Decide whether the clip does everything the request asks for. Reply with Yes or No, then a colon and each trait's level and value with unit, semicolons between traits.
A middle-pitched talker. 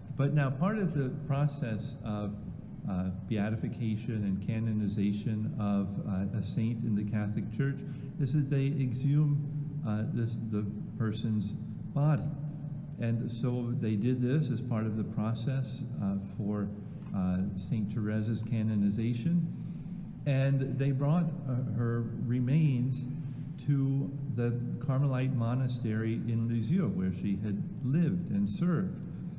No: low, 125 Hz